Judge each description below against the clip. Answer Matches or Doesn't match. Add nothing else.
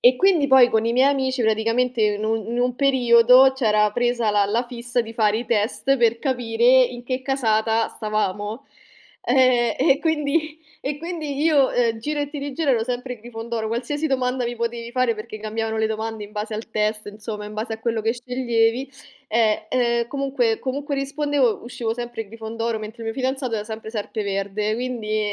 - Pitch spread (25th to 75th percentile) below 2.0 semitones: Doesn't match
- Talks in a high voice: Matches